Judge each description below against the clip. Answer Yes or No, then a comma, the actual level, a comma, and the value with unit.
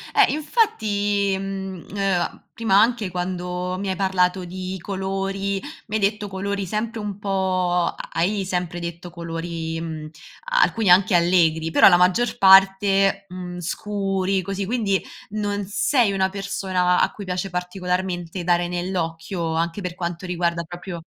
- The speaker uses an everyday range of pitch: No, narrow, 2.0 semitones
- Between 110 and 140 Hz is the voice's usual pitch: No, high, 190 Hz